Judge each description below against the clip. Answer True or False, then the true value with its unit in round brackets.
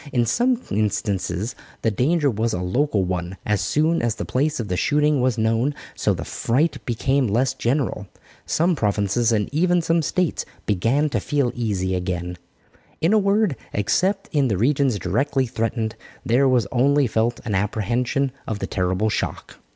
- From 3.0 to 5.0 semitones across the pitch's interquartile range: False (5.6 semitones)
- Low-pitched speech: True (120 Hz)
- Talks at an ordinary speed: True (165 wpm)